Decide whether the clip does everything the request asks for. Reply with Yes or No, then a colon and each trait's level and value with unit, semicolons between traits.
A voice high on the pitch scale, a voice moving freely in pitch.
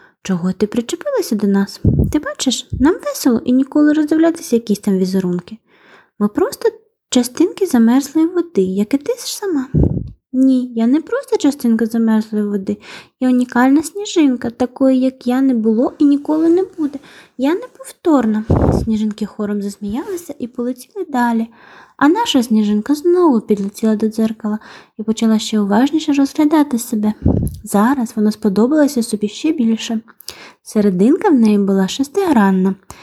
Yes: very high, 250 Hz; wide, 5.9 semitones